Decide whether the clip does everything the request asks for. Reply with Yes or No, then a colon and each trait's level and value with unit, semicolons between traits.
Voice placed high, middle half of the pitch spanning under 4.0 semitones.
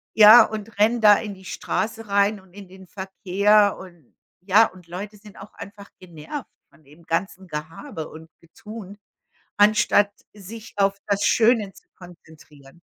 Yes: high, 200 Hz; average, 3.0 semitones